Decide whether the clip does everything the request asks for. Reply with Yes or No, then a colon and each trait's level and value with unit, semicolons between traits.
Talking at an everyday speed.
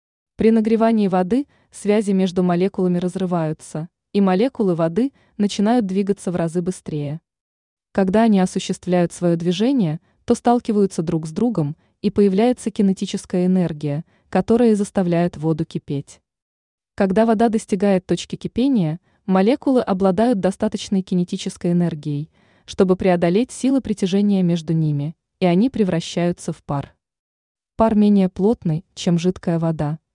Yes: average, 120 wpm